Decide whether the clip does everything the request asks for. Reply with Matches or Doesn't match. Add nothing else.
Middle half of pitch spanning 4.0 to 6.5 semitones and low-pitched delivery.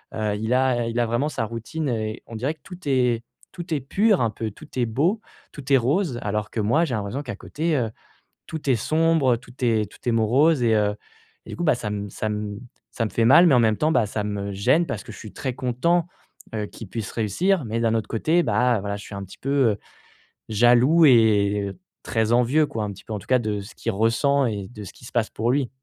Matches